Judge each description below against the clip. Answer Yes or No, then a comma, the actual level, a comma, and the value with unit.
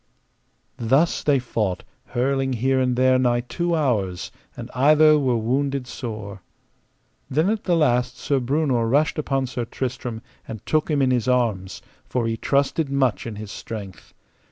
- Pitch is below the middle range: Yes, low, 130 Hz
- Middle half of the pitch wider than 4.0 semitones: No, average, 3.3 semitones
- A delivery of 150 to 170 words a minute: Yes, average, 155 wpm